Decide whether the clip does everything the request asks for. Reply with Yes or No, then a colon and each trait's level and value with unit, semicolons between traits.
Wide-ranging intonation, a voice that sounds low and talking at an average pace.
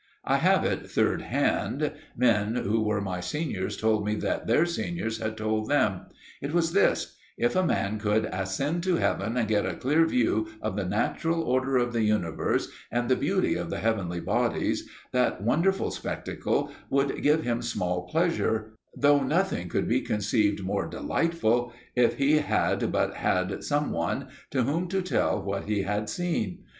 Yes: wide, 5.9 semitones; low, 115 Hz; average, 170 wpm